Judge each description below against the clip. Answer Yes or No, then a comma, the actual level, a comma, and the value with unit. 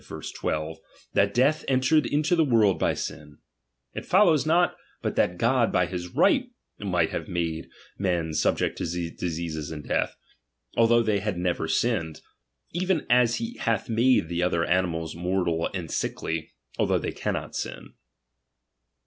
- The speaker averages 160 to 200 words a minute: No, average, 150 wpm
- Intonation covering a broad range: Yes, wide, 6.8 semitones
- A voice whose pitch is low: Yes, very low, 95 Hz